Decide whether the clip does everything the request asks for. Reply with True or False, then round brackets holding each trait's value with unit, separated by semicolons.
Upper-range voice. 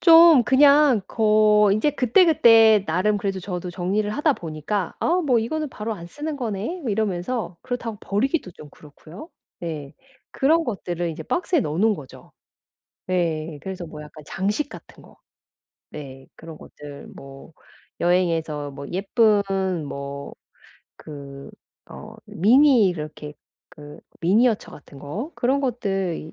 True (195 Hz)